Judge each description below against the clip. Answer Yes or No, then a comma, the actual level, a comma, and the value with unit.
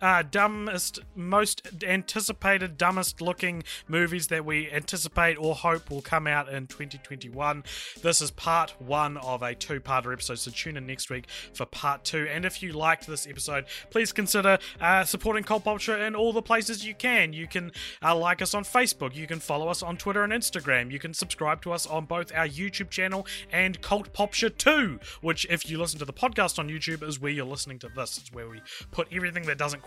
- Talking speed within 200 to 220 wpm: Yes, fast, 205 wpm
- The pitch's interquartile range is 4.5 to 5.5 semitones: Yes, average, 4.8 semitones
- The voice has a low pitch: No, medium, 170 Hz